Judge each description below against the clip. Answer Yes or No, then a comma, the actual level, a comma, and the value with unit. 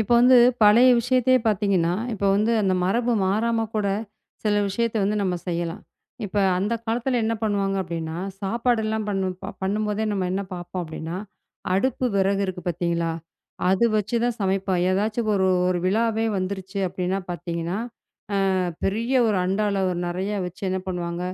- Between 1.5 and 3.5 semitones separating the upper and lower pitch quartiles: Yes, average, 3.2 semitones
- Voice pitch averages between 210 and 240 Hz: No, high, 200 Hz